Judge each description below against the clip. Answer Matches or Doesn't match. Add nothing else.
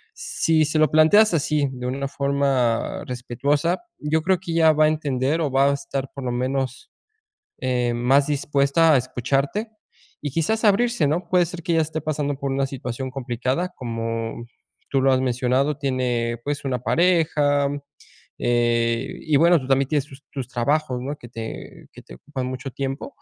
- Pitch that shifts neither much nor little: Matches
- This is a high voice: Doesn't match